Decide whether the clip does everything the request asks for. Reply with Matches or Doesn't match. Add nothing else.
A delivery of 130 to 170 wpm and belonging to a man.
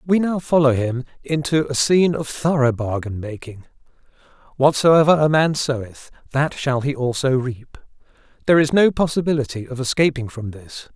Matches